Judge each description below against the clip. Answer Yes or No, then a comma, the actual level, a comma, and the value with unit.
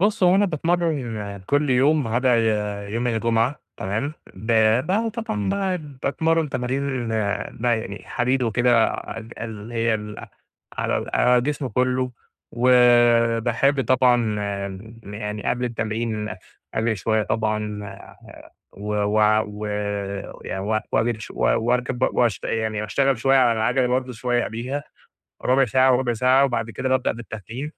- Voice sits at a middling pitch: No, low, 120 Hz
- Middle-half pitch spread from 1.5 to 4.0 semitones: Yes, average, 3.0 semitones